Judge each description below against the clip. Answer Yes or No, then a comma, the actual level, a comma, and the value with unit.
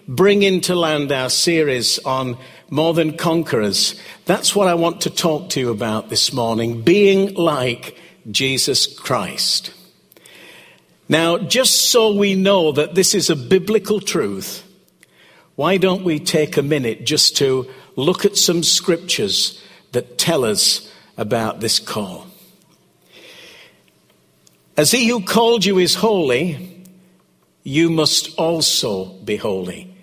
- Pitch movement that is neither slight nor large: No, wide, 5.9 semitones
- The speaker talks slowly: Yes, slow, 130 wpm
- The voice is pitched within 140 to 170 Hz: Yes, medium, 165 Hz